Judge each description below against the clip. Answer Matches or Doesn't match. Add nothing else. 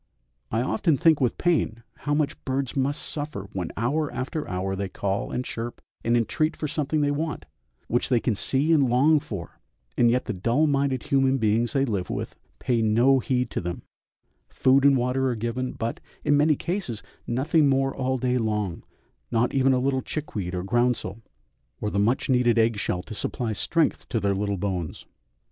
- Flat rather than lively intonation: Doesn't match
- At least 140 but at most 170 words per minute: Doesn't match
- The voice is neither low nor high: Doesn't match